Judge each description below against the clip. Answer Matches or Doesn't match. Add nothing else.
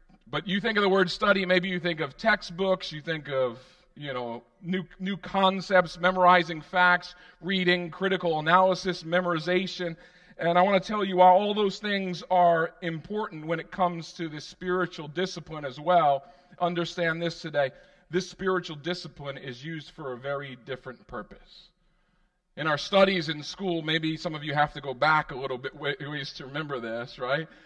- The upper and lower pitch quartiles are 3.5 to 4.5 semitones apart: Doesn't match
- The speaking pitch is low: Doesn't match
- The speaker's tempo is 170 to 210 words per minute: Matches